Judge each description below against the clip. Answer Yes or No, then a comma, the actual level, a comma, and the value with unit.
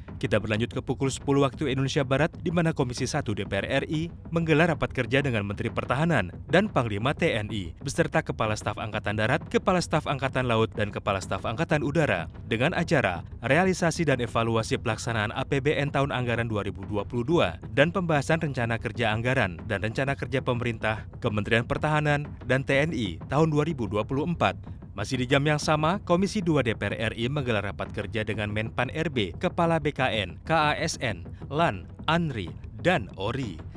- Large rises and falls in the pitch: Yes, wide, 5.8 semitones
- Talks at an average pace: No, fast, 150 wpm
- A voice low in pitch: Yes, low, 130 Hz